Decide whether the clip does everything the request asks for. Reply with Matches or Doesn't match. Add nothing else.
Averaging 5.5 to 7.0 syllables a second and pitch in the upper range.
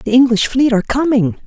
Matches